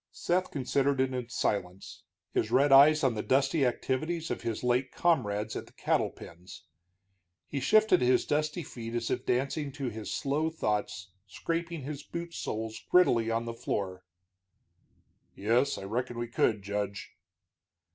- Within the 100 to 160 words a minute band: Yes, average, 155 wpm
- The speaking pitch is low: Yes, low, 125 Hz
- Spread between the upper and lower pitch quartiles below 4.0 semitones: No, average, 4.9 semitones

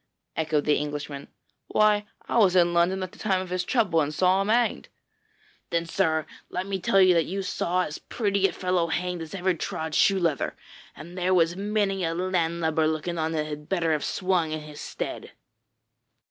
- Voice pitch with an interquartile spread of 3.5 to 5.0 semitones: No, average, 3.0 semitones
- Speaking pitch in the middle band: Yes, medium, 175 Hz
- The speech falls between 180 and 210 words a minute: Yes, average, 195 wpm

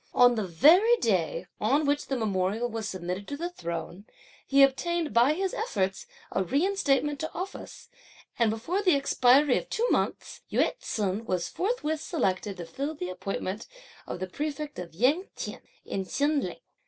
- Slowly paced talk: No, average, 165 wpm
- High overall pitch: Yes, very high, 255 Hz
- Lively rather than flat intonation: Yes, wide, 7.9 semitones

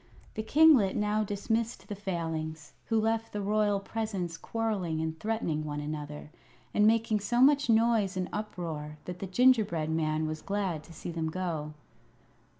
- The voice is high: Yes, high, 195 Hz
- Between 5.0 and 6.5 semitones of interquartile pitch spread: Yes, wide, 5.6 semitones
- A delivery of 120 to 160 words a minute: Yes, average, 155 wpm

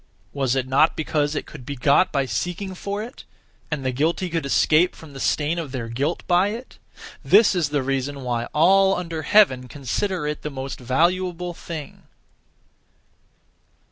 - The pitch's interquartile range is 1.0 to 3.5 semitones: No, average, 4.7 semitones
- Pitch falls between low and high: Yes, medium, 150 Hz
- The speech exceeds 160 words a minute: Yes, average, 170 wpm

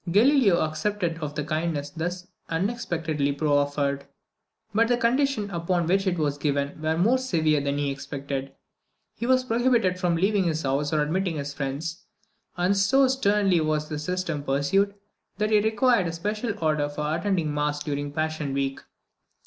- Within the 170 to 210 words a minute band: No, average, 160 wpm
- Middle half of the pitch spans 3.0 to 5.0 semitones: No, wide, 5.4 semitones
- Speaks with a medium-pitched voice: Yes, medium, 165 Hz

